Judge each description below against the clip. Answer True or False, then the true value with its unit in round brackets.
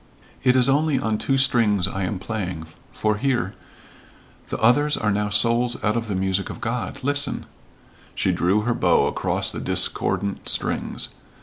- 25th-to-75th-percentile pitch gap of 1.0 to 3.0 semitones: False (4.1 semitones)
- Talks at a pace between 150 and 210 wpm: True (170 wpm)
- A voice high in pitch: False (110 Hz)